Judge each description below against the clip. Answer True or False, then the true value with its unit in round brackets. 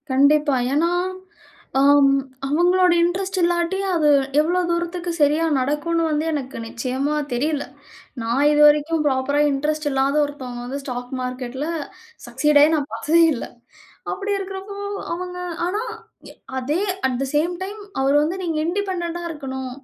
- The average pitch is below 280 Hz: False (300 Hz)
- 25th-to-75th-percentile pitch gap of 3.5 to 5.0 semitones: True (4.1 semitones)